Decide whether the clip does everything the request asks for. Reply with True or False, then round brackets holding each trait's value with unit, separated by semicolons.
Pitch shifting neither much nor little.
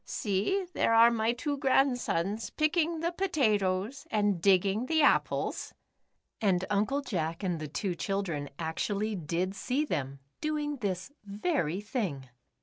False (7.1 semitones)